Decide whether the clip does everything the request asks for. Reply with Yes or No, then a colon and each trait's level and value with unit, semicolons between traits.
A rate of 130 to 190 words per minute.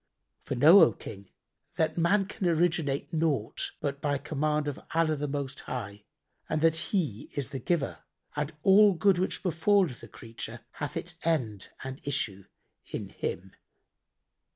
Yes: average, 155 wpm